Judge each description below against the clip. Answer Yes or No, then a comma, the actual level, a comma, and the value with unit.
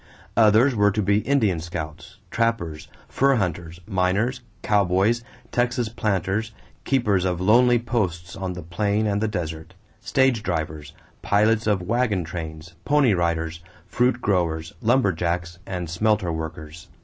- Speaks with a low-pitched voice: Yes, very low, 95 Hz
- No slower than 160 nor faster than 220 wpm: No, slow, 135 wpm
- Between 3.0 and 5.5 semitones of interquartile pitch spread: Yes, average, 5.0 semitones